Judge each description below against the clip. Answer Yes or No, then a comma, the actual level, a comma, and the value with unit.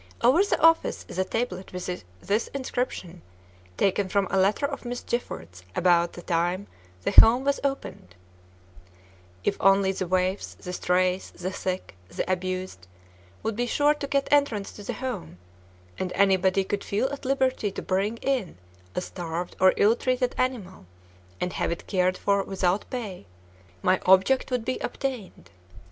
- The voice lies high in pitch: Yes, high, 195 Hz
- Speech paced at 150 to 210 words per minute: Yes, average, 160 wpm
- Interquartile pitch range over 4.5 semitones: Yes, average, 5.2 semitones